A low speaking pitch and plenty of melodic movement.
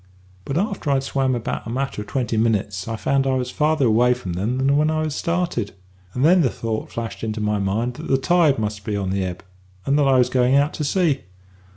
No: low, 125 Hz; average, 4.5 semitones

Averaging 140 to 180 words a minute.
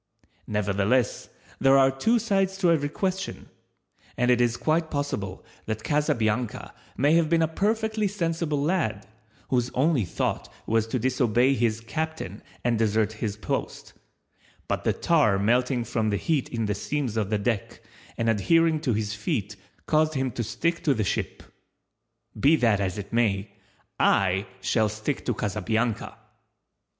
Yes: average, 155 wpm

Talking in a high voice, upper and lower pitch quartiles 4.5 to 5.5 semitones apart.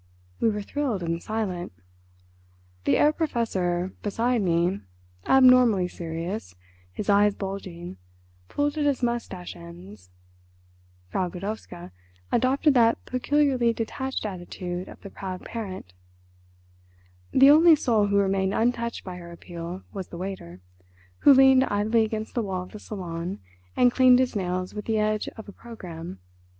Yes: high, 205 Hz; average, 5.0 semitones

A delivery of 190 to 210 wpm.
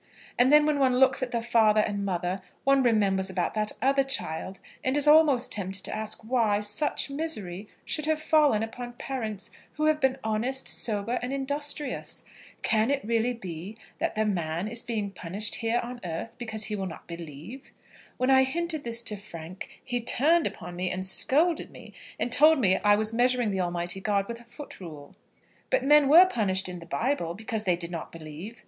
Yes: average, 195 wpm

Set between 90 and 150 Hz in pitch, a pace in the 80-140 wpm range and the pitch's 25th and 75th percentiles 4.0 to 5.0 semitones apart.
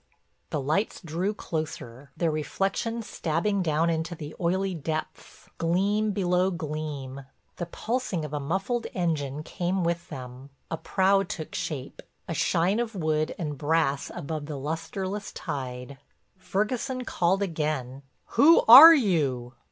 No: medium, 165 Hz; slow, 135 wpm; average, 4.6 semitones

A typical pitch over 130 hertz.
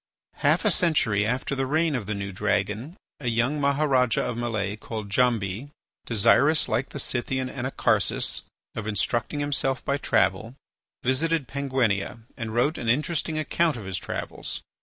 No: low, 125 Hz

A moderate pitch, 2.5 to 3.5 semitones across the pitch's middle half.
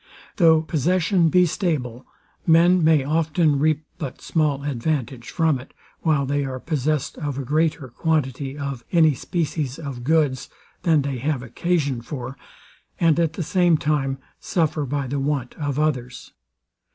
Yes: medium, 150 Hz; average, 3.1 semitones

